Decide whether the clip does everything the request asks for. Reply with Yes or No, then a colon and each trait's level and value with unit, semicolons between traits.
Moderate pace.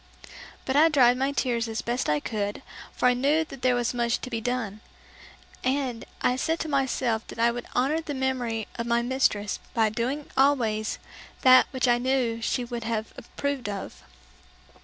Yes: average, 180 wpm